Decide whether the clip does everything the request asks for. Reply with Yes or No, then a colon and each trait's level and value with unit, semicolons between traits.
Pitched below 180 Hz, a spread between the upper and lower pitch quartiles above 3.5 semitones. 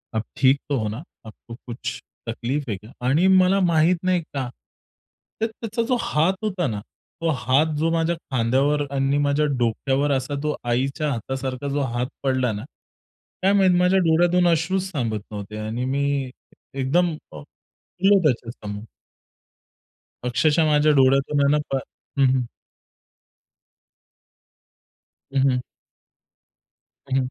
Yes: medium, 140 Hz; average, 4.6 semitones